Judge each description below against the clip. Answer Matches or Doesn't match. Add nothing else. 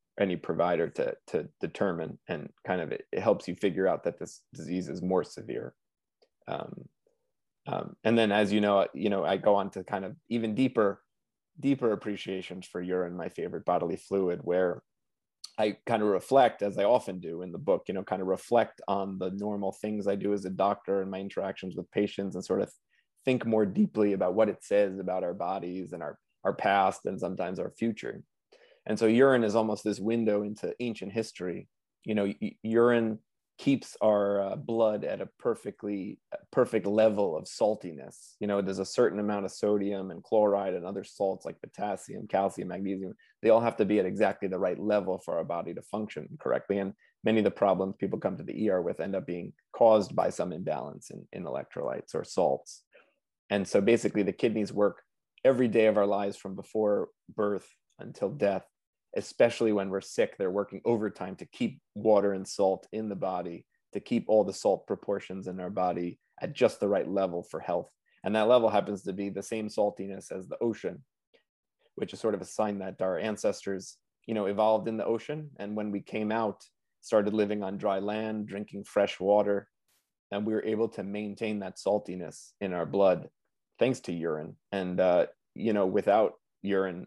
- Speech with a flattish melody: Matches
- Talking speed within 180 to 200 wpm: Matches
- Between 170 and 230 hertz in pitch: Doesn't match